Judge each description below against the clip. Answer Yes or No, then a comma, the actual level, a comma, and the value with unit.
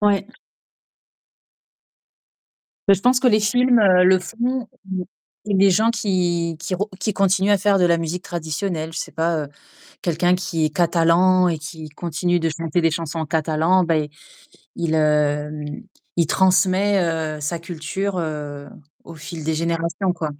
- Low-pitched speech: No, medium, 175 Hz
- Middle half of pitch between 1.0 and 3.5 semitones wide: Yes, average, 3.1 semitones